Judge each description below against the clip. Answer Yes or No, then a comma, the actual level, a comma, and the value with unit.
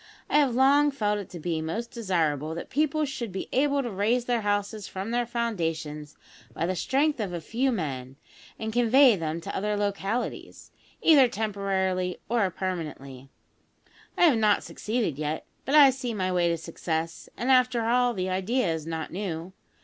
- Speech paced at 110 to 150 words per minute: No, average, 175 wpm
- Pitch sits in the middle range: No, high, 205 Hz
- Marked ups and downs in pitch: Yes, wide, 6.4 semitones